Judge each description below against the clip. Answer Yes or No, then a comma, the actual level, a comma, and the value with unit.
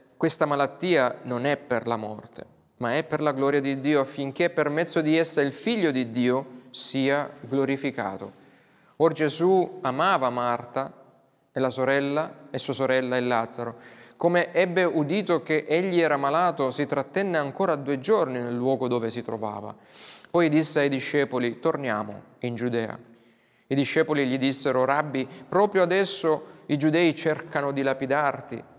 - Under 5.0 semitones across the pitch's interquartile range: Yes, average, 3.8 semitones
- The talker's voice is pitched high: No, medium, 140 Hz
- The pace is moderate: Yes, average, 150 wpm